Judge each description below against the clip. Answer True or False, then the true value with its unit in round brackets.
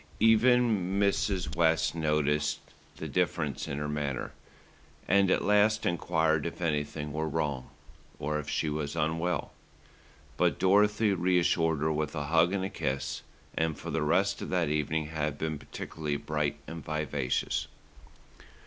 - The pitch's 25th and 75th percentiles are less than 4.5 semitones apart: True (3.4 semitones)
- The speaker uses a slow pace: False (145 wpm)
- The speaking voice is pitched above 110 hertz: False (80 Hz)